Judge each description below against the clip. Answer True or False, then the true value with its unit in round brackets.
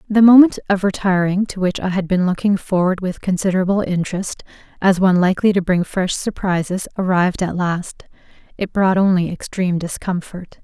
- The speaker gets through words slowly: False (165 wpm)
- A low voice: False (185 Hz)